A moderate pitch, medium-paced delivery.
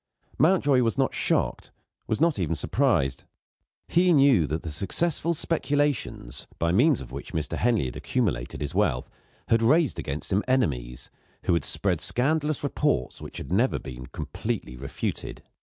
No: low, 115 Hz; average, 155 wpm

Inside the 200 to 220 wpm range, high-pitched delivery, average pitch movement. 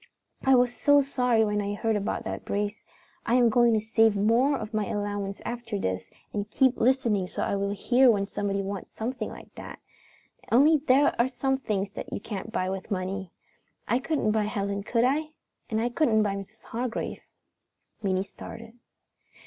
No: average, 180 wpm; high, 220 Hz; average, 3.6 semitones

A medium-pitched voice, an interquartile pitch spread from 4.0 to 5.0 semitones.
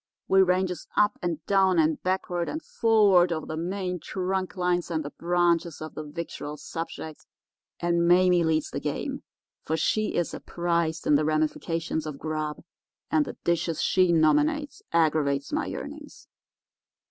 No: medium, 170 Hz; average, 2.9 semitones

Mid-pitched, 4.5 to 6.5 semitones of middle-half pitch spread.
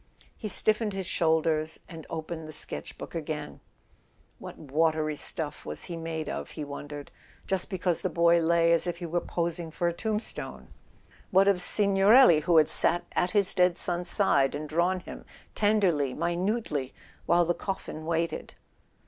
No: medium, 170 Hz; average, 2.8 semitones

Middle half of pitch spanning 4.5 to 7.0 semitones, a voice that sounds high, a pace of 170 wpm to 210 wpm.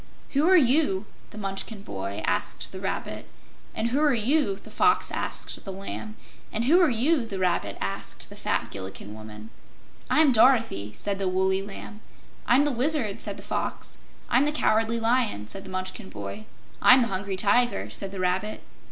Yes: average, 5.2 semitones; high, 210 Hz; average, 180 wpm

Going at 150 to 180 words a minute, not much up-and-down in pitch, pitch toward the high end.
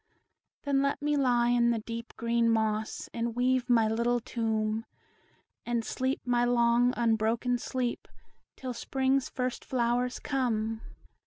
No: slow, 135 wpm; narrow, 1.6 semitones; high, 240 Hz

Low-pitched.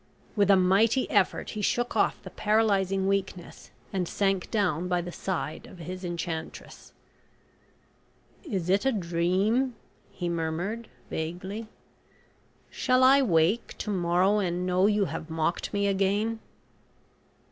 No: high, 190 Hz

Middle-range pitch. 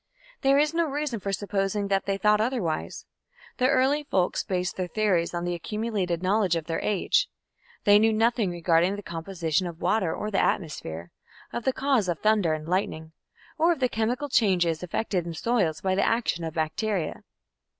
No: high, 195 Hz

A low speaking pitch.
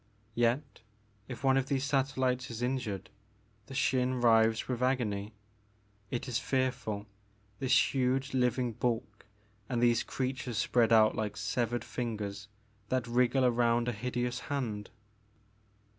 Yes: low, 120 Hz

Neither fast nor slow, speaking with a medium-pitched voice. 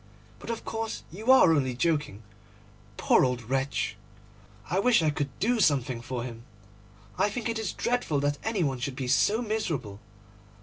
Yes: average, 170 wpm; medium, 150 Hz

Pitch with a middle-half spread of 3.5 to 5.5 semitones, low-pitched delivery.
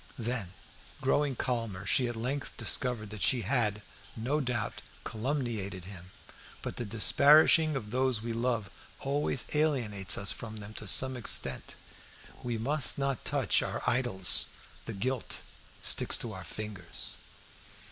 Yes: average, 3.8 semitones; low, 120 Hz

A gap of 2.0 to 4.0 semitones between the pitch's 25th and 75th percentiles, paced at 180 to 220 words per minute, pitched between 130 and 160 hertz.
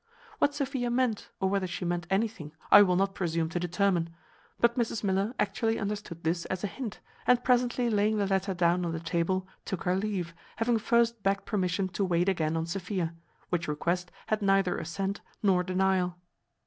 No: average, 3.3 semitones; average, 185 wpm; high, 190 Hz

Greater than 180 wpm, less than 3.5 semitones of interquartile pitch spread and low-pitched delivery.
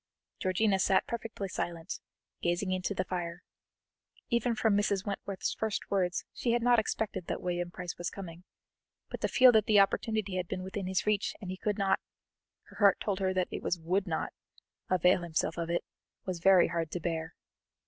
No: average, 190 wpm; average, 2.8 semitones; medium, 185 Hz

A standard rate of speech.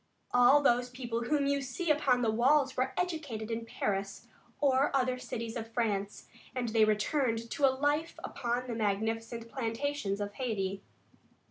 Yes: average, 155 wpm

